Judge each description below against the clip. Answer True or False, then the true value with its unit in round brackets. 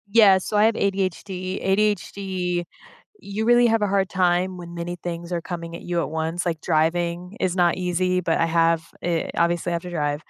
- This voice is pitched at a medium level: True (180 Hz)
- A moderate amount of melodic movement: False (2.1 semitones)